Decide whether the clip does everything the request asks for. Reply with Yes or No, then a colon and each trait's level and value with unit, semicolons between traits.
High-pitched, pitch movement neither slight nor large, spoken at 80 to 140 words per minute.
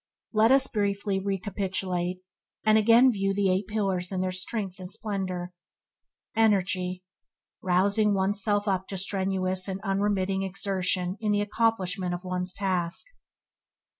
No: high, 195 Hz; narrow, 1.9 semitones; slow, 135 wpm